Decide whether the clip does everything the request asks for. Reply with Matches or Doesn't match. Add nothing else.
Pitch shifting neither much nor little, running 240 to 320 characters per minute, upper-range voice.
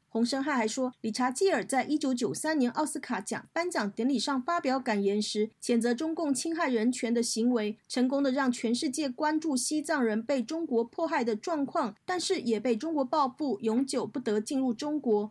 Matches